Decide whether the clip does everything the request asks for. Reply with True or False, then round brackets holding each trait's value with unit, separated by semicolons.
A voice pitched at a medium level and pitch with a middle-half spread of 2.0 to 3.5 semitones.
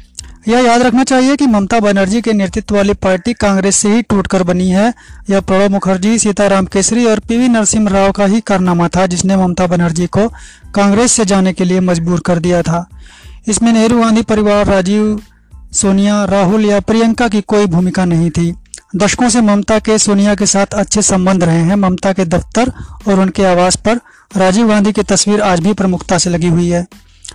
False (200 Hz; 2.6 semitones)